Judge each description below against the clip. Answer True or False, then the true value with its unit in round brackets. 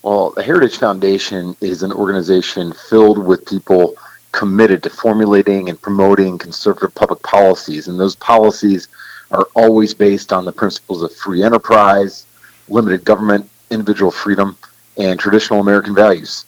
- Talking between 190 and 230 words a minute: False (140 wpm)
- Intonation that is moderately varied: False (1.8 semitones)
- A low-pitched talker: True (100 Hz)